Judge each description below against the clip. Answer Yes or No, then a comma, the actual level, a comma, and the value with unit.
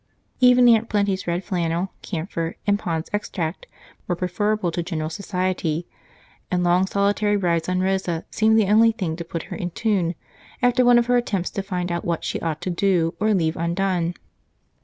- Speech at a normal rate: Yes, average, 180 wpm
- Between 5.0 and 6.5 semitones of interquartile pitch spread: No, average, 3.4 semitones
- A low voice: No, medium, 185 Hz